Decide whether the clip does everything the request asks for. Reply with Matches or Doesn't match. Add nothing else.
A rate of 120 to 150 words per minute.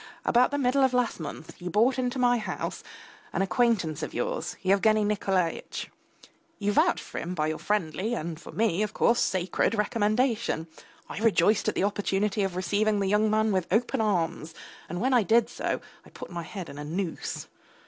Doesn't match